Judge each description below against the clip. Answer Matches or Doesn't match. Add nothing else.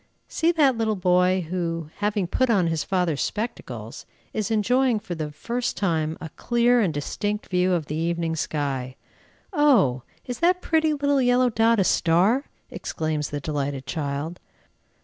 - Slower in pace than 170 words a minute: Matches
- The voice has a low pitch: Doesn't match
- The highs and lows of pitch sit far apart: Matches